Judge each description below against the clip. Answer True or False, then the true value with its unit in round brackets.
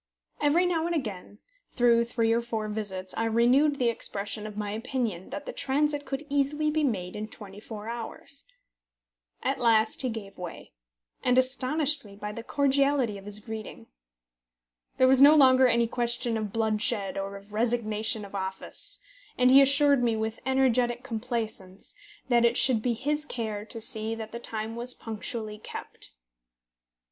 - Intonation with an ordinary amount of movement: True (3.6 semitones)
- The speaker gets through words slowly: False (165 wpm)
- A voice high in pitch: True (235 Hz)